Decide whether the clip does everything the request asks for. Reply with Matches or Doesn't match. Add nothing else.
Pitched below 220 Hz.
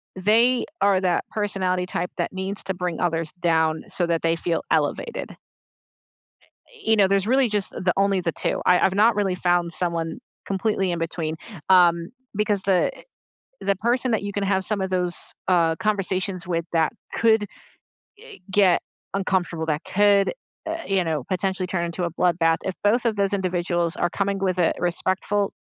Matches